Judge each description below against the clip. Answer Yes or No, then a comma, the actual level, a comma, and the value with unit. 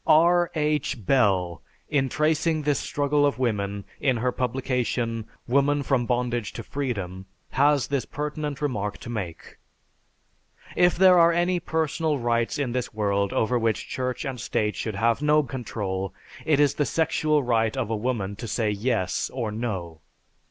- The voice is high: No, low, 125 Hz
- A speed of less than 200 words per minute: Yes, average, 160 wpm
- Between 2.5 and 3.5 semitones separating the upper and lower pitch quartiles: No, average, 5.1 semitones